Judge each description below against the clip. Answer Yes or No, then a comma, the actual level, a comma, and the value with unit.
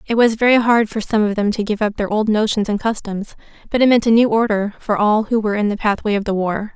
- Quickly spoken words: Yes, fast, 285 wpm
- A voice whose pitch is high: Yes, high, 215 Hz